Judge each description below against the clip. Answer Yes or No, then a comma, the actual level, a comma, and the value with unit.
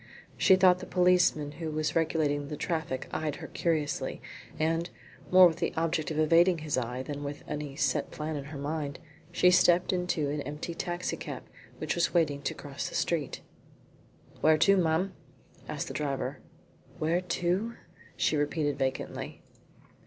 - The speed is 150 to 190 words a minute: Yes, average, 160 wpm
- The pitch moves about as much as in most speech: Yes, average, 3.1 semitones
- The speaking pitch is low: No, medium, 155 Hz